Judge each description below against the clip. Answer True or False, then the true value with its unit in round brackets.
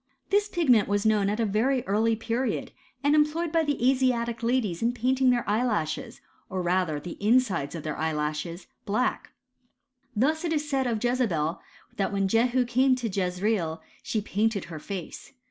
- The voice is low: False (225 Hz)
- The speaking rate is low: False (165 wpm)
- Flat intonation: False (5.3 semitones)